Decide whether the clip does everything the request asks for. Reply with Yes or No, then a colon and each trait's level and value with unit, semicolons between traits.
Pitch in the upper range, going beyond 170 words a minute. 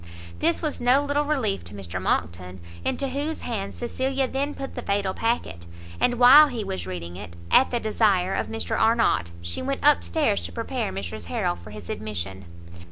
Yes: high, 195 Hz; average, 185 wpm